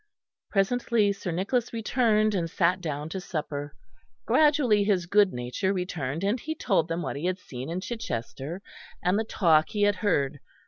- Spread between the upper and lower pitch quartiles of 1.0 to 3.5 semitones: No, average, 4.8 semitones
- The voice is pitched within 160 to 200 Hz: Yes, medium, 185 Hz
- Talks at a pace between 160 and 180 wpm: Yes, average, 170 wpm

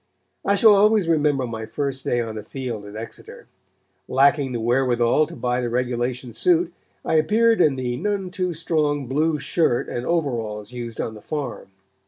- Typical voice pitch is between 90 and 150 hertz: Yes, low, 135 Hz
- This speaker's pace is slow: No, average, 175 wpm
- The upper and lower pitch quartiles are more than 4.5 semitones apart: Yes, average, 5.3 semitones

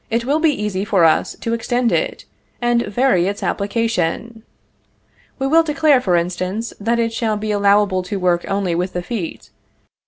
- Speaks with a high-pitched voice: Yes, high, 210 Hz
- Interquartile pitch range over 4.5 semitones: No, average, 4.2 semitones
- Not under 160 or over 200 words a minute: Yes, average, 180 wpm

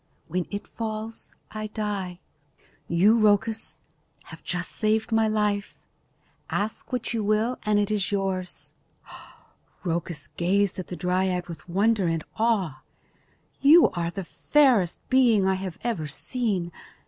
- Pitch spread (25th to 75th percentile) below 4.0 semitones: Yes, average, 3.5 semitones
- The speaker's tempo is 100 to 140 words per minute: Yes, slow, 135 wpm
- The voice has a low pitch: No, high, 205 Hz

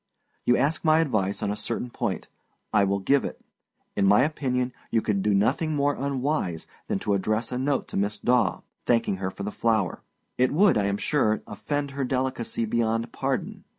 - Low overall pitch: Yes, low, 115 Hz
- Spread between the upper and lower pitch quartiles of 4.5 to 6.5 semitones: Yes, average, 5.2 semitones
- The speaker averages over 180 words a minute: Yes, average, 190 wpm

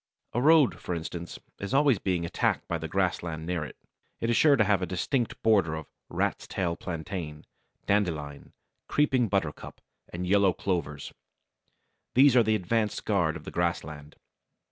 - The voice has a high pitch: No, very low, 90 Hz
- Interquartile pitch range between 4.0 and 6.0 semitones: Yes, average, 5.0 semitones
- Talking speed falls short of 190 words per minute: Yes, average, 160 wpm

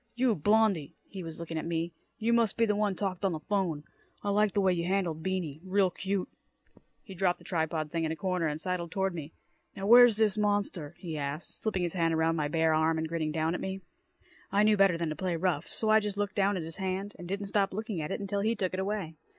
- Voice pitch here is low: No, medium, 185 Hz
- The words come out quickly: Yes, fast, 250 wpm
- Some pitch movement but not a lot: Yes, average, 3.8 semitones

